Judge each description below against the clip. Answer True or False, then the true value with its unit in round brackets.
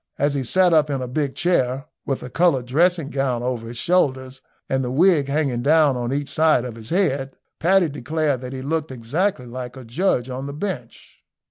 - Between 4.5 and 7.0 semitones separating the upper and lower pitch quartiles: False (3.9 semitones)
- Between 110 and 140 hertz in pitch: True (135 Hz)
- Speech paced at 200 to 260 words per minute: True (205 wpm)